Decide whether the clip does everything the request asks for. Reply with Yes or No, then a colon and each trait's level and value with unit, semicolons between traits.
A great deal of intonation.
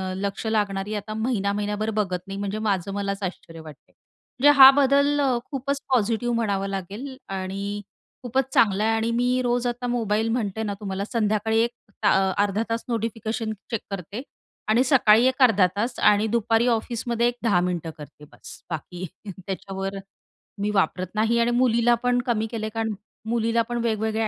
No: average, 3.2 semitones